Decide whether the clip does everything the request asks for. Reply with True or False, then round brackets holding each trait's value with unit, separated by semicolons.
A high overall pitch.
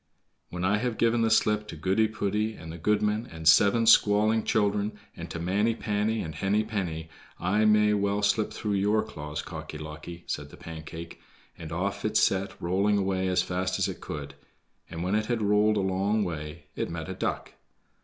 False (100 Hz)